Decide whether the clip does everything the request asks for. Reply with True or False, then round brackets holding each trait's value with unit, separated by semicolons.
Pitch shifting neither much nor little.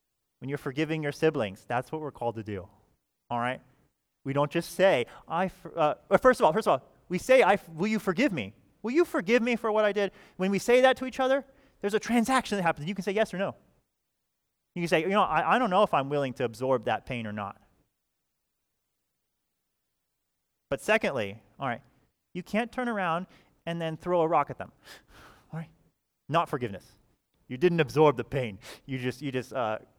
False (7.7 semitones)